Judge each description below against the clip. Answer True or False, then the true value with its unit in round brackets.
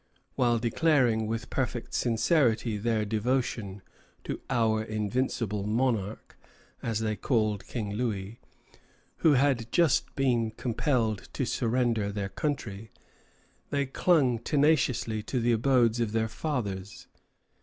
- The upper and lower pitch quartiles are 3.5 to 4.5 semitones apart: False (3.1 semitones)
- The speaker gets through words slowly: True (115 wpm)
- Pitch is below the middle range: True (115 Hz)